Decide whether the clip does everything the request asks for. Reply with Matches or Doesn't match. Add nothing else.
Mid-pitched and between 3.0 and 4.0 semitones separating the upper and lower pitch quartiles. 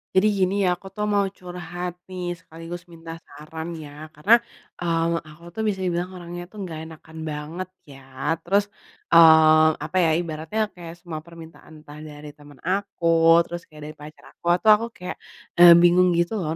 Doesn't match